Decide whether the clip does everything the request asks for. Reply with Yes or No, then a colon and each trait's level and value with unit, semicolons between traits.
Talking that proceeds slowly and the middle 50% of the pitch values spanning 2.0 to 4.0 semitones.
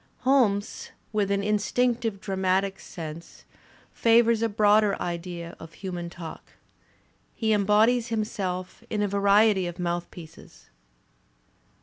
Yes: slow, 110 wpm; average, 3.4 semitones